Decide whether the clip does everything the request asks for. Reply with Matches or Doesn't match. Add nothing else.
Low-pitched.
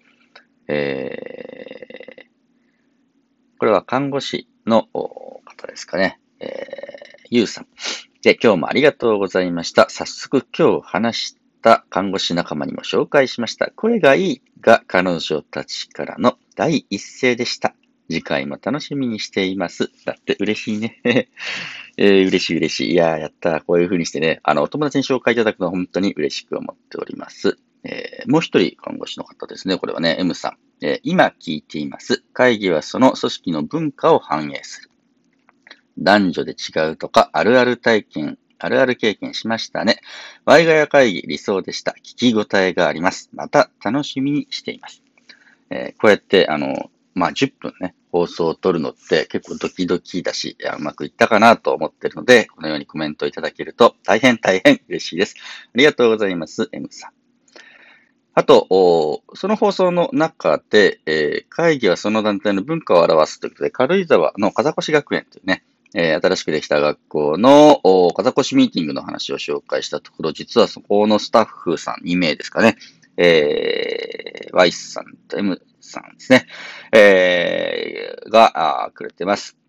Doesn't match